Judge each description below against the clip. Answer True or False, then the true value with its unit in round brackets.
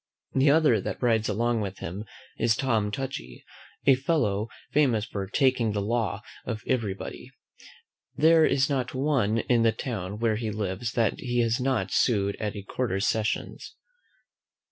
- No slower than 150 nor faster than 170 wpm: True (160 wpm)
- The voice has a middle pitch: False (115 Hz)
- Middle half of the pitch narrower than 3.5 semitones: False (3.9 semitones)